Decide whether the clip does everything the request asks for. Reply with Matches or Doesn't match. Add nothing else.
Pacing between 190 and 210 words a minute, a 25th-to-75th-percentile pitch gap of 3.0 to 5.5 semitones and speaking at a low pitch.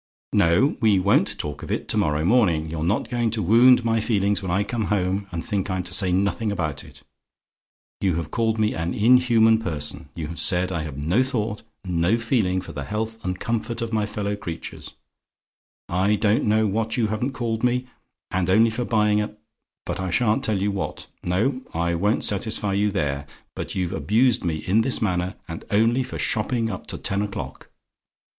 Matches